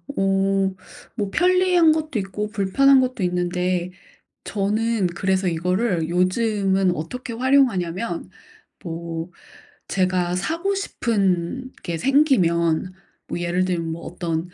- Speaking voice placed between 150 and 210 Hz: Yes, high, 190 Hz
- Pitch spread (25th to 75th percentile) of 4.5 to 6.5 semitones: Yes, average, 5.1 semitones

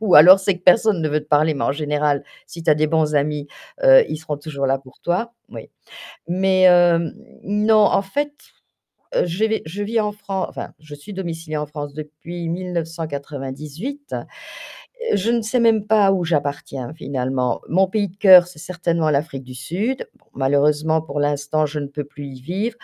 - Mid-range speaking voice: Yes, medium, 160 Hz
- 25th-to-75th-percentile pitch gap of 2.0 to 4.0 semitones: No, average, 4.7 semitones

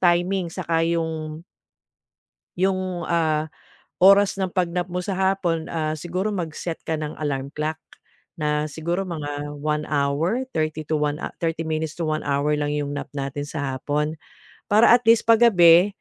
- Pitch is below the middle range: No, medium, 160 Hz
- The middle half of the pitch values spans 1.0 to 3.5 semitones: Yes, average, 3.1 semitones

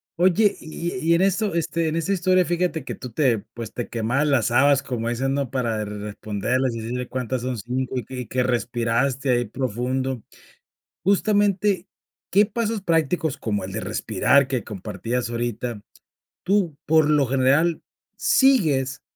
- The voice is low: Yes, low, 130 Hz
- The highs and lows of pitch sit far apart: Yes, wide, 5.9 semitones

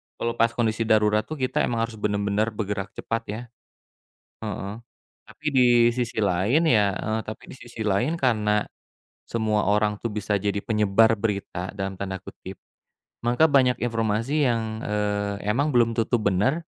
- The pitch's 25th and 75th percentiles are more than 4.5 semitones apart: No, narrow, 2.4 semitones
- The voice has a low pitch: Yes, low, 110 Hz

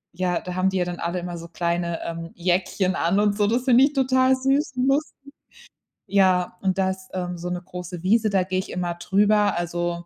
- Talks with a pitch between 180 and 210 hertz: Yes, medium, 185 Hz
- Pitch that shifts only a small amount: No, average, 3.0 semitones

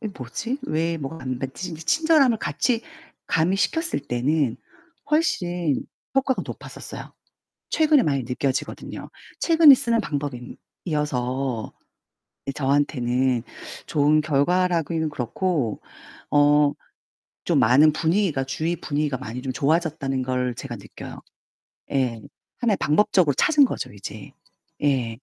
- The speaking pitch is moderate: Yes, medium, 150 Hz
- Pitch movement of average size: No, wide, 5.7 semitones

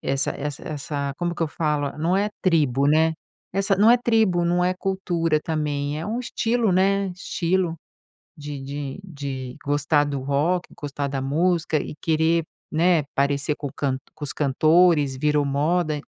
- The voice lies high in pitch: No, medium, 155 Hz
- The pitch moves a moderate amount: Yes, average, 3.8 semitones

